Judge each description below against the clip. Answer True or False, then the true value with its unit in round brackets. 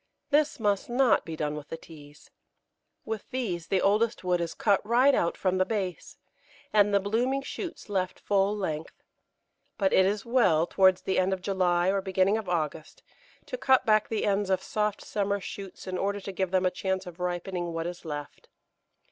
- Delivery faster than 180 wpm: True (190 wpm)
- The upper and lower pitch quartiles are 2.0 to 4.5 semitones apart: True (2.9 semitones)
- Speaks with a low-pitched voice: False (190 Hz)